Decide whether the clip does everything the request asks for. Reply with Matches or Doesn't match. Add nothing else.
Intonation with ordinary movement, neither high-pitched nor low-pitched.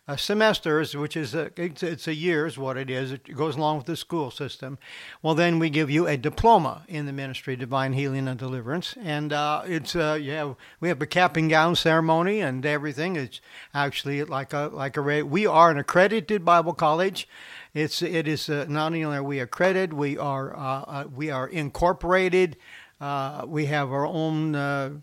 Matches